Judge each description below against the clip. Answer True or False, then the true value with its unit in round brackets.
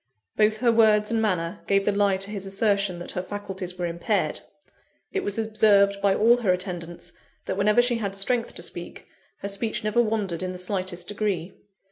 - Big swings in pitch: False (2.7 semitones)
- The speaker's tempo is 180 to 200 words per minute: True (190 wpm)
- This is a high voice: True (200 Hz)